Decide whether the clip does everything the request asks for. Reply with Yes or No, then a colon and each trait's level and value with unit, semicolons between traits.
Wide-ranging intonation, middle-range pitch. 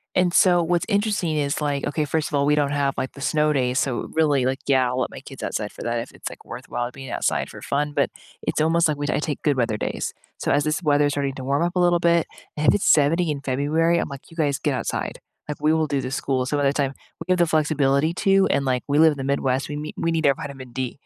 No: average, 2.8 semitones; medium, 145 Hz